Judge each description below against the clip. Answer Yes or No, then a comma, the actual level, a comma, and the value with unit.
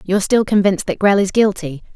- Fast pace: Yes, fast, 215 wpm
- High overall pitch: Yes, high, 195 Hz